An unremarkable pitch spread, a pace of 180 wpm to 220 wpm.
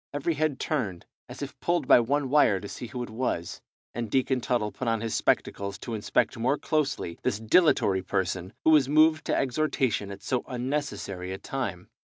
No: wide, 5.9 semitones; average, 190 wpm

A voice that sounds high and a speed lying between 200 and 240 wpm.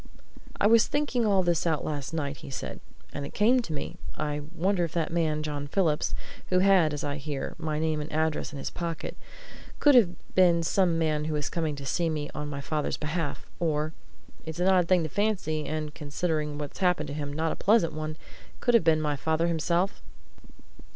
No: medium, 160 Hz; fast, 205 wpm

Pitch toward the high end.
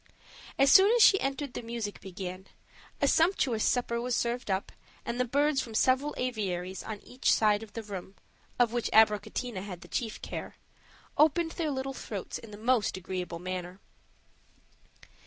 Yes: high, 230 Hz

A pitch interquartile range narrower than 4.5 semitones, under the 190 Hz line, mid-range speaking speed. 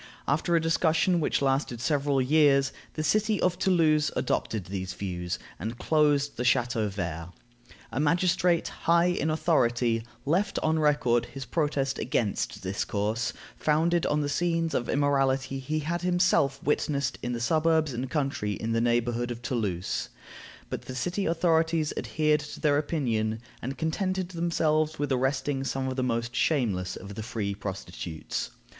No: average, 5.1 semitones; medium, 140 Hz; average, 155 wpm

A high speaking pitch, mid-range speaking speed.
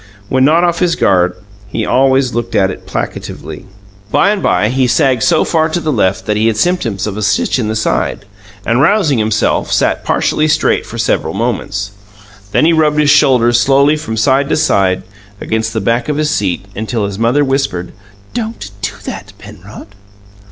No: low, 125 Hz; average, 185 wpm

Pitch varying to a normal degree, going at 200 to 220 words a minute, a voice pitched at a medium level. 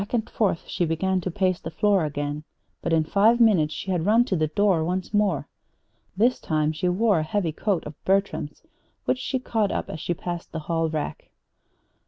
Yes: average, 4.4 semitones; fast, 205 wpm; medium, 180 Hz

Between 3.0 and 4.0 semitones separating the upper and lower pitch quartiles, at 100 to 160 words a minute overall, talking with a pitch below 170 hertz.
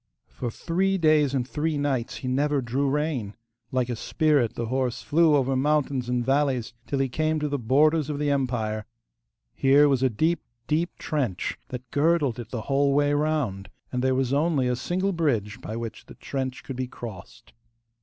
No: average, 3.3 semitones; average, 185 wpm; low, 135 Hz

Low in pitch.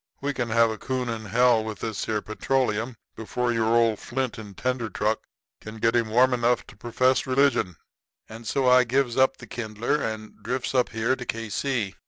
Yes: low, 115 Hz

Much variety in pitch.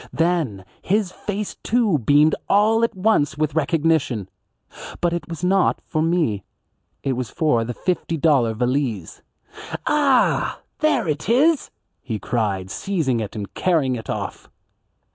Yes: wide, 7.6 semitones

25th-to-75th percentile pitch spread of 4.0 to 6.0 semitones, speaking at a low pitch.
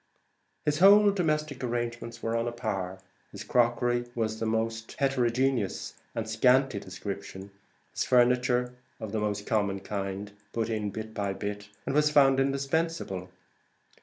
Yes: average, 4.3 semitones; low, 115 Hz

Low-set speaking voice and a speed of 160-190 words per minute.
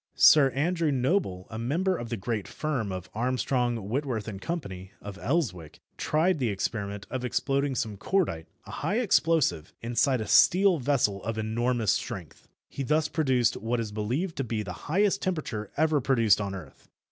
Yes: low, 125 Hz; average, 170 wpm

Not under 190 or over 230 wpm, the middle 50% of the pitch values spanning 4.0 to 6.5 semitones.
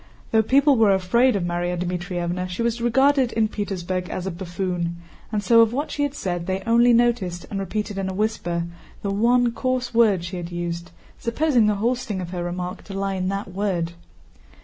Yes: average, 200 wpm; average, 4.7 semitones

